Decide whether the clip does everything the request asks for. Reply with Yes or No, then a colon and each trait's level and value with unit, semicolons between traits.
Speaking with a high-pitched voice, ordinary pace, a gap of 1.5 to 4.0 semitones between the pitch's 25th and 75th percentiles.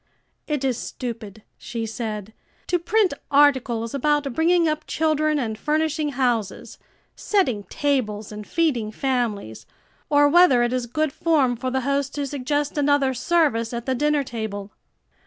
No: very high, 265 Hz; average, 145 wpm; average, 4.5 semitones